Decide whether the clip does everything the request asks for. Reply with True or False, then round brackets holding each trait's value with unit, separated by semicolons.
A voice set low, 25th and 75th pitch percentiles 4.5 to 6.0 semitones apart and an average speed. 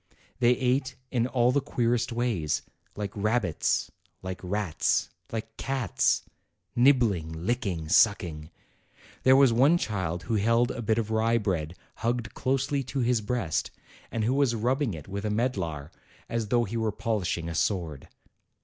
True (115 Hz; 4.8 semitones; 150 wpm)